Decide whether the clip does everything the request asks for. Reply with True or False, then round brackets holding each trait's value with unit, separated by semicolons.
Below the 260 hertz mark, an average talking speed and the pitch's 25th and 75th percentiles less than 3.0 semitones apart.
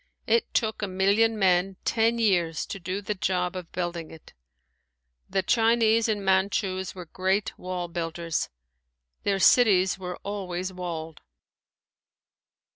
False (190 Hz; 125 wpm; 2.5 semitones)